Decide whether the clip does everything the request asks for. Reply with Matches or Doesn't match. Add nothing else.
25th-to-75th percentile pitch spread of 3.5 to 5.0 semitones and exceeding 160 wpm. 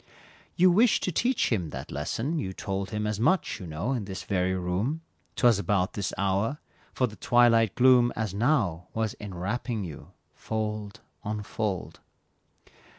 Doesn't match